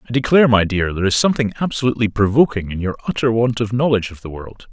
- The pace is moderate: No, fast, 230 wpm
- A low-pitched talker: Yes, low, 110 Hz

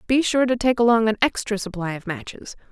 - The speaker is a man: No, female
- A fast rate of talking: Yes, fast, 220 wpm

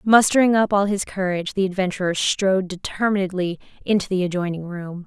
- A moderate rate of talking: Yes, average, 155 wpm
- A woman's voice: Yes, female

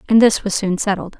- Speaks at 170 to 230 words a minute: No, fast, 250 wpm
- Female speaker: Yes, female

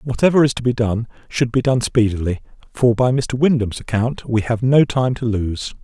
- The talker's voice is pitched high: No, low, 120 Hz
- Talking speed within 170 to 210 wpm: Yes, fast, 205 wpm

